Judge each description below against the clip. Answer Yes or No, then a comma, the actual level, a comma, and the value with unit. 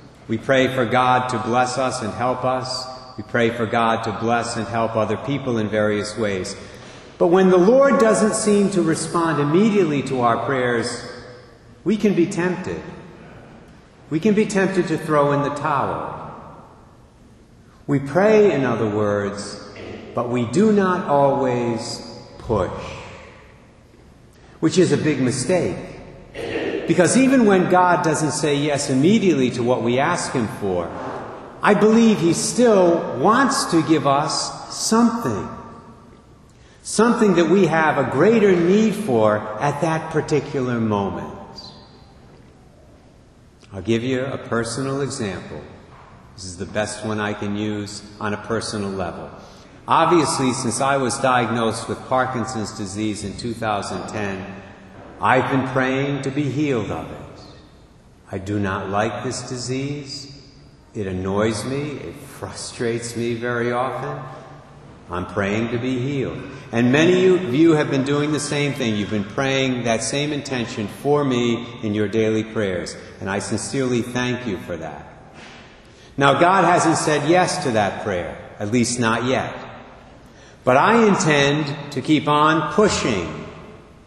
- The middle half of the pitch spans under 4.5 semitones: No, wide, 5.4 semitones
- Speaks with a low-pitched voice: Yes, low, 130 Hz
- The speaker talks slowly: No, average, 145 wpm